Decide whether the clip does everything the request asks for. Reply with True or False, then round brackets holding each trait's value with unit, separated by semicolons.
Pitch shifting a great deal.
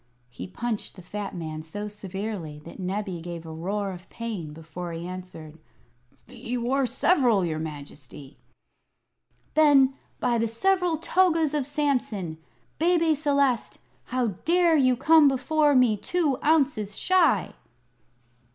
True (8.3 semitones)